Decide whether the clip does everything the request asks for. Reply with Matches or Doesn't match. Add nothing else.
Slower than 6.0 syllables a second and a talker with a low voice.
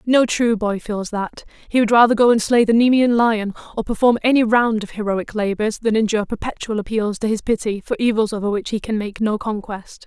Doesn't match